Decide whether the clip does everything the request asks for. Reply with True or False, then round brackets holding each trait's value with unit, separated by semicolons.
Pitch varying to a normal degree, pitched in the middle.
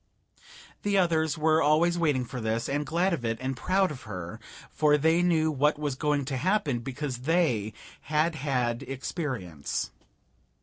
True (4.4 semitones; 150 Hz)